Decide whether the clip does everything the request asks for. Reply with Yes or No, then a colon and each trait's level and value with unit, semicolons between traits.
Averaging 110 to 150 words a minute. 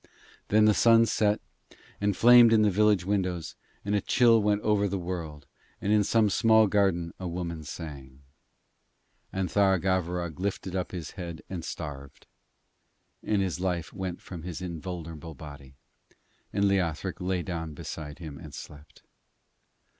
Yes: average, 145 wpm